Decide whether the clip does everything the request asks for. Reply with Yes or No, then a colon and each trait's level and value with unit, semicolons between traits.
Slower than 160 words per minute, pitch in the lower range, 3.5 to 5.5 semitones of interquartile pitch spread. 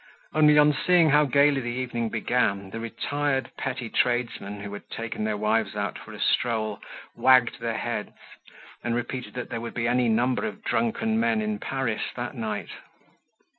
No: average, 170 wpm; low, 120 Hz; average, 4.2 semitones